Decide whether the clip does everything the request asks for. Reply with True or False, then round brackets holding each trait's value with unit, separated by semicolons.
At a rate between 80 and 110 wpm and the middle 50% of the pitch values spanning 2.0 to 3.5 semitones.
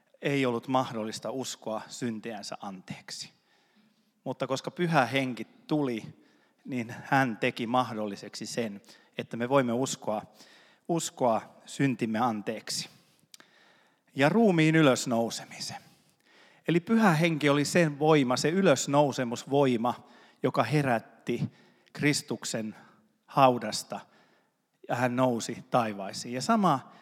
False (100 wpm; 4.1 semitones)